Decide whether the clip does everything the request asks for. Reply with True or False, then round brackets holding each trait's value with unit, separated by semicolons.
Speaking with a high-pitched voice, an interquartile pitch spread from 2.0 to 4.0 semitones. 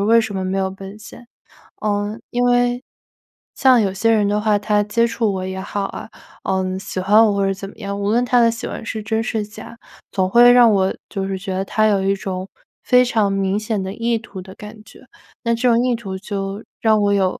True (210 Hz; 2.8 semitones)